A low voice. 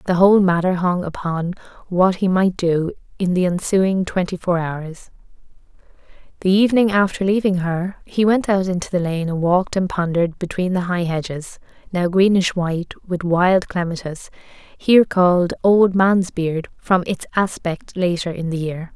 No: medium, 180 Hz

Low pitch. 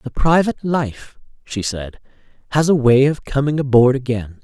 Yes: low, 130 Hz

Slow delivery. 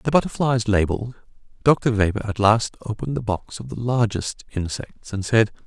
No: average, 170 wpm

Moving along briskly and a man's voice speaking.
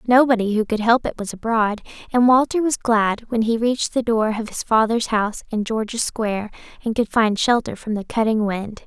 No: fast, 210 wpm; female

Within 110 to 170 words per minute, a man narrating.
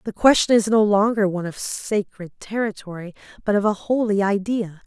No: average, 160 wpm; female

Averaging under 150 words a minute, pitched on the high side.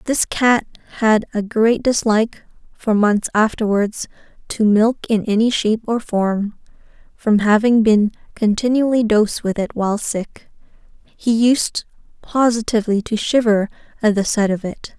Yes: average, 140 wpm; high, 220 Hz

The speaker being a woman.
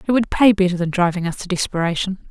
Yes: female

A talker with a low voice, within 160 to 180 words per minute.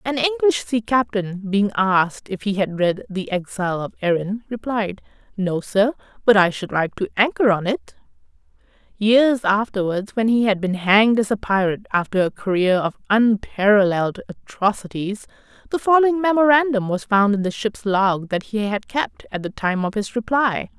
No: high, 210 Hz; average, 175 wpm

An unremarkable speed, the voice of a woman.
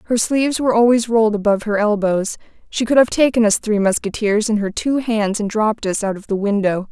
No: fast, 225 wpm; female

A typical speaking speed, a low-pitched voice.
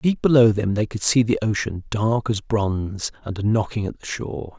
No: fast, 210 wpm; low, 110 Hz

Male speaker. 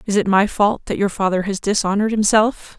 No: female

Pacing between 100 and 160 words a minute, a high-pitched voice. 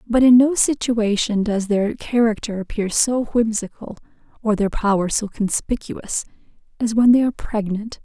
Yes: average, 150 wpm; high, 220 Hz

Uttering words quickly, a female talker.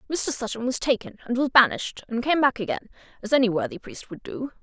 Yes: fast, 220 wpm; female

